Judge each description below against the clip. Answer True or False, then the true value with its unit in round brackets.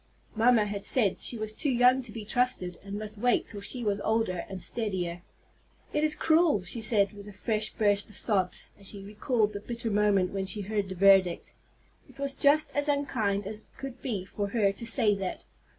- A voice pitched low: False (210 Hz)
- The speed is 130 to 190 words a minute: False (205 wpm)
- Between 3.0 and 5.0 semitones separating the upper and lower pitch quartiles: True (3.4 semitones)